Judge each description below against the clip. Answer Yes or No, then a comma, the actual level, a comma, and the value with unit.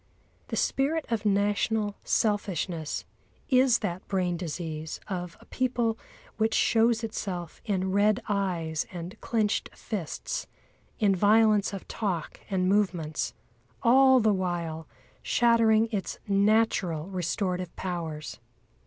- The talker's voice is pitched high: Yes, high, 200 Hz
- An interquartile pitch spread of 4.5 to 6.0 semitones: No, average, 3.9 semitones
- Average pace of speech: No, slow, 110 wpm